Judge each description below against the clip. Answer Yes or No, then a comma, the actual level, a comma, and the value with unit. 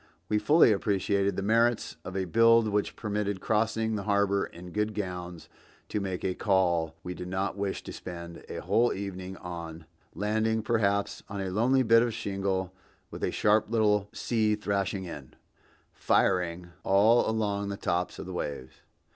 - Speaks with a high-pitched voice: No, low, 100 Hz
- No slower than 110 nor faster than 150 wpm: No, average, 165 wpm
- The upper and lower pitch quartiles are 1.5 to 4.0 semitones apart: Yes, average, 2.8 semitones